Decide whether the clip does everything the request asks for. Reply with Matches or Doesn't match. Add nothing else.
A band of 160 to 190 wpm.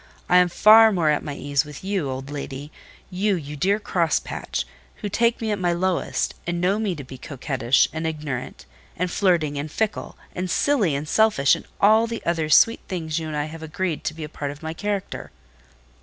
Doesn't match